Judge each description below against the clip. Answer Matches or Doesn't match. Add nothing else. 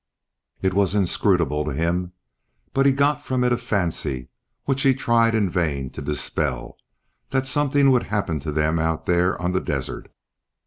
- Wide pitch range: Matches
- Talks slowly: Doesn't match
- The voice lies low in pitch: Matches